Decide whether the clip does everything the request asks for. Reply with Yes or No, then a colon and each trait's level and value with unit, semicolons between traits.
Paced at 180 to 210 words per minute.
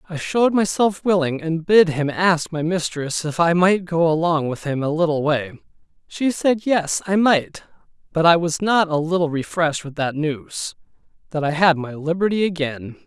Yes: average, 190 wpm